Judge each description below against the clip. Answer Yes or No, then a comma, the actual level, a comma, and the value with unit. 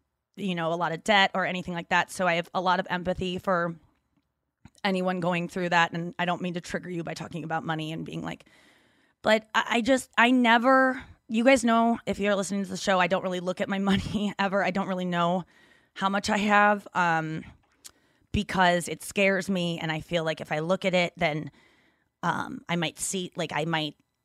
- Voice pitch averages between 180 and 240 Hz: Yes, medium, 185 Hz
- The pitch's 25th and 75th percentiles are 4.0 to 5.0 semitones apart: No, average, 2.8 semitones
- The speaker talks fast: Yes, fast, 220 wpm